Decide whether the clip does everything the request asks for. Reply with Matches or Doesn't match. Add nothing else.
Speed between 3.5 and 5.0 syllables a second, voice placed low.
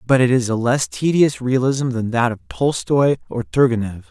Matches